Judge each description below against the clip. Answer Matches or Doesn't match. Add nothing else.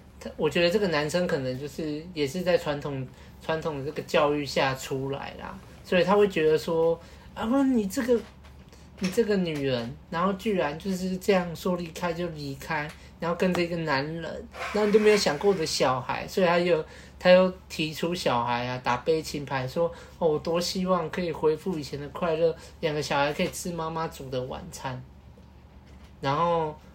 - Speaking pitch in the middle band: Matches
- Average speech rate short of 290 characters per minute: Matches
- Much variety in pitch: Doesn't match